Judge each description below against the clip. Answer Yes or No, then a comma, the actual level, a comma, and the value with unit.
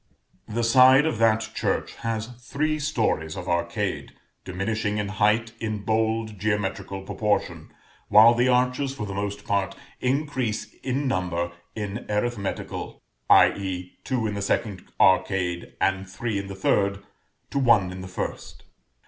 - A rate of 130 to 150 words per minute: Yes, average, 140 wpm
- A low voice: Yes, low, 105 Hz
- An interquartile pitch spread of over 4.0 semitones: No, average, 3.4 semitones